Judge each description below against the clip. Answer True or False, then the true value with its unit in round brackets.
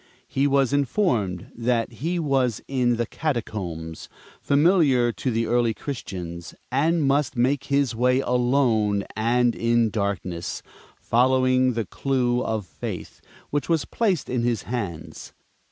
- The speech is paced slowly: True (130 wpm)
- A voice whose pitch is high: False (125 Hz)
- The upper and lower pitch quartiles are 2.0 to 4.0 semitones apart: True (3.7 semitones)